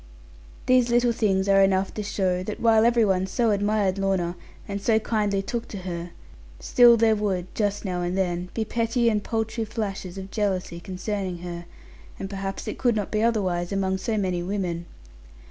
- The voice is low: No, high, 200 Hz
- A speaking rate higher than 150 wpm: Yes, average, 180 wpm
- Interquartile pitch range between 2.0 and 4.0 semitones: Yes, average, 2.9 semitones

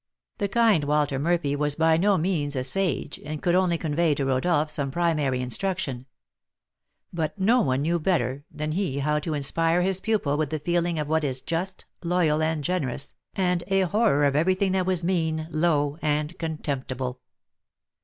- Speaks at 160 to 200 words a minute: Yes, average, 175 wpm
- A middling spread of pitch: Yes, average, 3.7 semitones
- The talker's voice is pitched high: No, medium, 160 Hz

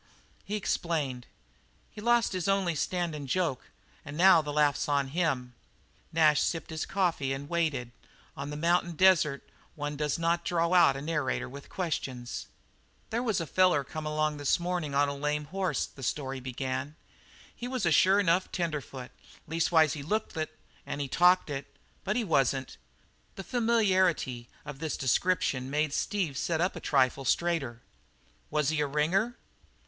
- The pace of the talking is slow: No, average, 165 wpm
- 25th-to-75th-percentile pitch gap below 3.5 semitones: No, average, 4.2 semitones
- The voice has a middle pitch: Yes, medium, 155 Hz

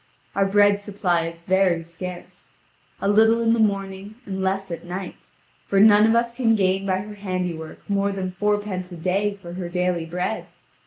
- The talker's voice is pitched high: Yes, high, 195 Hz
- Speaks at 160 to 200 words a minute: Yes, average, 180 wpm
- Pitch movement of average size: No, narrow, 2.2 semitones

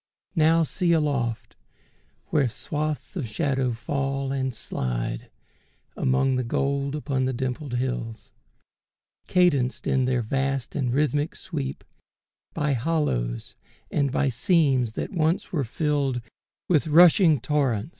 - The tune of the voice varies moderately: Yes, average, 3.3 semitones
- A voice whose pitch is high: No, low, 135 Hz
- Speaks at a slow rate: Yes, slow, 120 wpm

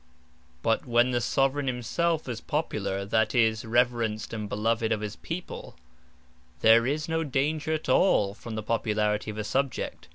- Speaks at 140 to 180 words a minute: Yes, average, 160 wpm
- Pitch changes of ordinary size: Yes, average, 4.2 semitones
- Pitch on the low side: Yes, low, 115 Hz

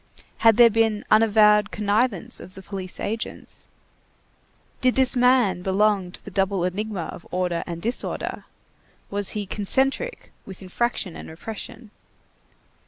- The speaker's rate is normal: No, slow, 130 wpm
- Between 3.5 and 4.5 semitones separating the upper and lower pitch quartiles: No, average, 3.1 semitones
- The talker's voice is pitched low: No, high, 210 Hz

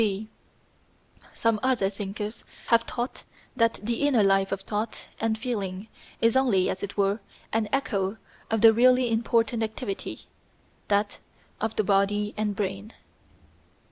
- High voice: Yes, high, 215 Hz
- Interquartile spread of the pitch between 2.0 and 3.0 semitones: Yes, narrow, 2.5 semitones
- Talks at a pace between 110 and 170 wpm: Yes, average, 140 wpm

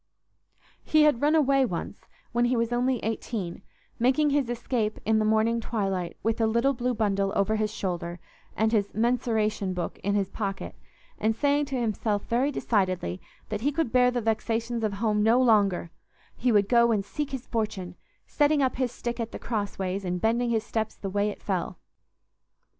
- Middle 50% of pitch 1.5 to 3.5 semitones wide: Yes, average, 3.2 semitones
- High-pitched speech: Yes, high, 225 Hz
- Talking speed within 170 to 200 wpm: Yes, average, 180 wpm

